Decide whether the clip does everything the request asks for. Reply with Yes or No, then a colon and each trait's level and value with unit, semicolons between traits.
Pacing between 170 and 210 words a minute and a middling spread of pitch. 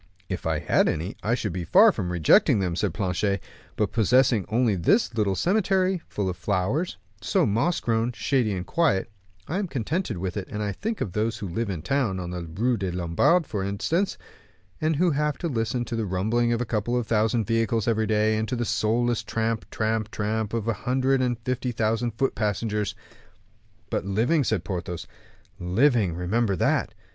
Yes: average, 190 wpm; average, 4.1 semitones